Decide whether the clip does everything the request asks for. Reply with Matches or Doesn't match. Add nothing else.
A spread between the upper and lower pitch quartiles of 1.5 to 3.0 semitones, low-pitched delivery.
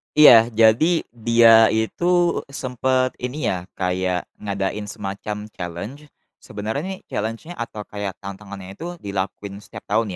Doesn't match